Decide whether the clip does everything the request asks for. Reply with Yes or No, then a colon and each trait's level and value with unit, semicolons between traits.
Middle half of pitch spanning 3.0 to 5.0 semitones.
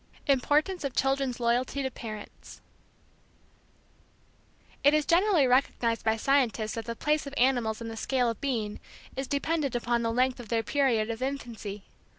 Yes: average, 3.5 semitones